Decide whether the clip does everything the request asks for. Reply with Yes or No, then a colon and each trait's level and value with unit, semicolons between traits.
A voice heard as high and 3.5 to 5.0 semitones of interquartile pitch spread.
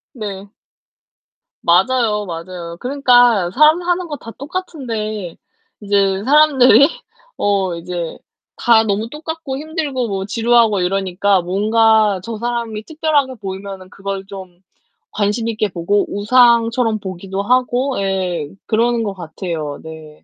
Yes: high, 215 Hz; average, 4.5 semitones